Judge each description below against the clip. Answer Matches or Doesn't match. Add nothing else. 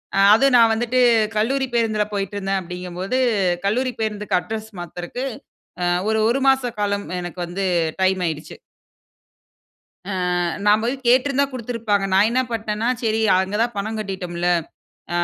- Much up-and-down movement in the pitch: Doesn't match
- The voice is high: Matches